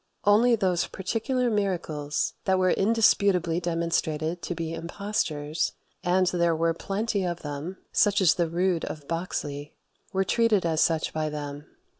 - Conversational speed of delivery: Yes, average, 145 wpm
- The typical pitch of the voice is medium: Yes, medium, 175 Hz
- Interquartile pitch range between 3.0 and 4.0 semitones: Yes, average, 3.5 semitones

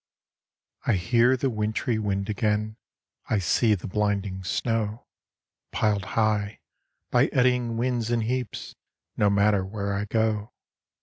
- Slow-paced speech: Yes, slow, 125 wpm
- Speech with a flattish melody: Yes, narrow, 2.3 semitones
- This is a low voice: Yes, low, 105 Hz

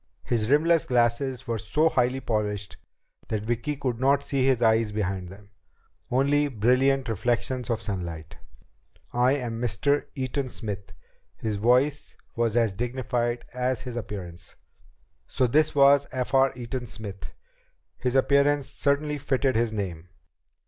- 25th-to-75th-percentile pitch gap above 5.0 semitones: No, average, 3.7 semitones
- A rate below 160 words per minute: Yes, slow, 135 wpm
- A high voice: No, low, 120 Hz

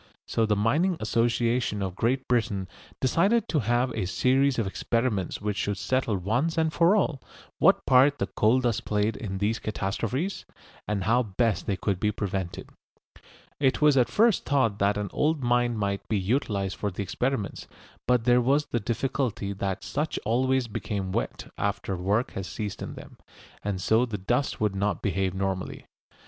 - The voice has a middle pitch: No, low, 115 Hz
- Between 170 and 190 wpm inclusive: Yes, average, 175 wpm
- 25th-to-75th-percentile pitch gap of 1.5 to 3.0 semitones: No, average, 4.5 semitones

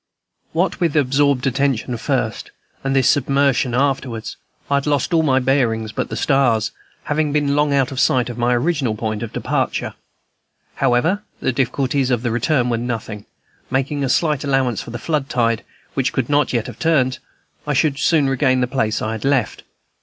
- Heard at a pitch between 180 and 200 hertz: No, low, 135 Hz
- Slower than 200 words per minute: Yes, average, 180 wpm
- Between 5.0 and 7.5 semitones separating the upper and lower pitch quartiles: No, average, 2.8 semitones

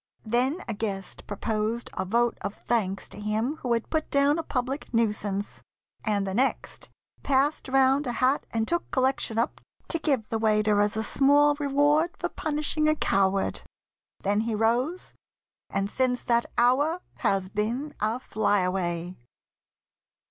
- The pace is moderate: Yes, average, 155 wpm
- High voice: Yes, high, 235 Hz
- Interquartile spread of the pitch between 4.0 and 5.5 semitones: Yes, average, 5.0 semitones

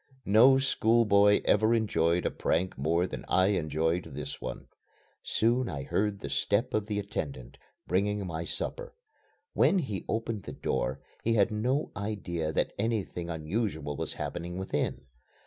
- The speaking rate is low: No, average, 145 wpm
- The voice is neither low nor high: No, low, 100 Hz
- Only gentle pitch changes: No, average, 5.0 semitones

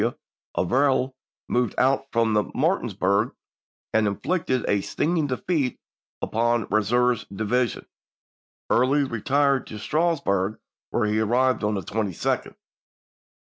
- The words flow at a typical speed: No, slow, 115 wpm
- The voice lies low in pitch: Yes, low, 120 Hz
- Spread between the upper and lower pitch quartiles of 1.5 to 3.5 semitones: No, average, 3.9 semitones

